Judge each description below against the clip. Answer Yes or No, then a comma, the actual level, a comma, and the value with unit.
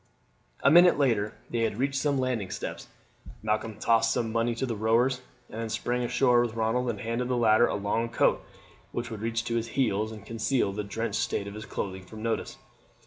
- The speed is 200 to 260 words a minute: Yes, fast, 205 wpm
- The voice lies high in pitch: No, low, 115 Hz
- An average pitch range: No, narrow, 2.1 semitones